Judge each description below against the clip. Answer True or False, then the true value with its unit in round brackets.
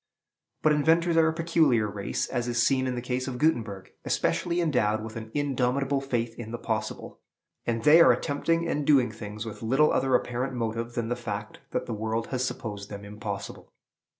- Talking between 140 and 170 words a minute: False (195 wpm)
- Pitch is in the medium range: False (120 Hz)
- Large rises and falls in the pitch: False (4.2 semitones)